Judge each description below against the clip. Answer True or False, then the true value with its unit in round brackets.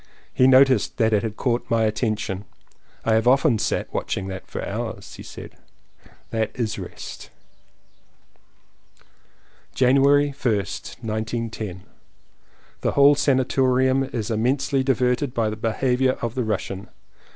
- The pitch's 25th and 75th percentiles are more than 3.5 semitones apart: False (3.2 semitones)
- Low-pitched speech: True (120 Hz)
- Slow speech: True (130 wpm)